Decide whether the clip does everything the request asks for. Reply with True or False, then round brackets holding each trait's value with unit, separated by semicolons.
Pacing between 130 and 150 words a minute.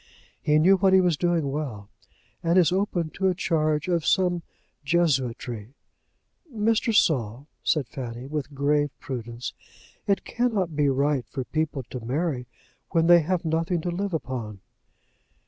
True (145 wpm)